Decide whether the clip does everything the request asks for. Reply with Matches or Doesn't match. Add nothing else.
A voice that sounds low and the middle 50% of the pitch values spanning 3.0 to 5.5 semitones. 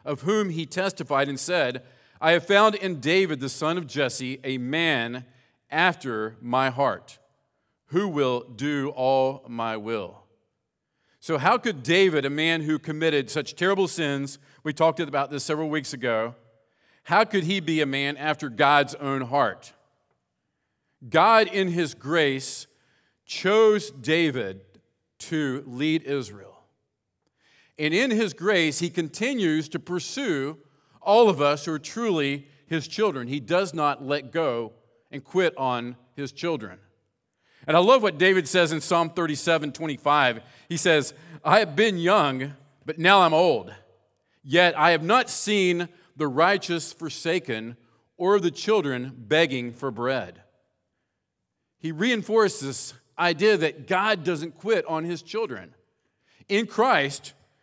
Doesn't match